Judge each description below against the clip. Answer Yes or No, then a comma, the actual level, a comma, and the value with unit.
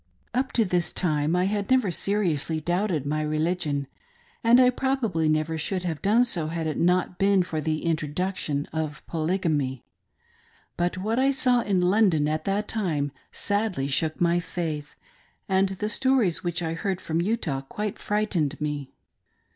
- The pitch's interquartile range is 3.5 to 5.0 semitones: Yes, average, 4.7 semitones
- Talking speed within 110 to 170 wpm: Yes, average, 160 wpm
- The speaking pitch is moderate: Yes, medium, 175 Hz